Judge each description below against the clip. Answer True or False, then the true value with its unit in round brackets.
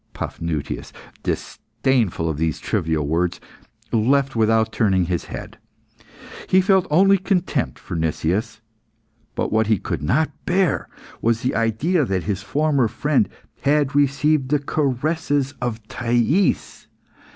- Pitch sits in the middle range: False (120 Hz)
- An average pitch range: False (6.9 semitones)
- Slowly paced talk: True (125 wpm)